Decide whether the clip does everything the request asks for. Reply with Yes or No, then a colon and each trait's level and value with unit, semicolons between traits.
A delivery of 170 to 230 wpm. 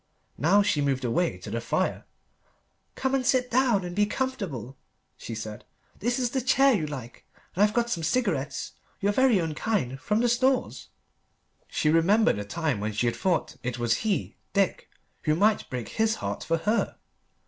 Yes: average, 185 wpm